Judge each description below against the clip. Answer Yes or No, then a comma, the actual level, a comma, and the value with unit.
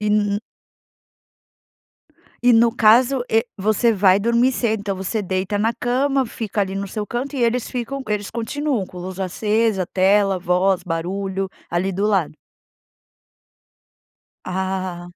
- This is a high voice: Yes, high, 205 Hz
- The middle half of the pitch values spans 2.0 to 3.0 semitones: No, average, 3.6 semitones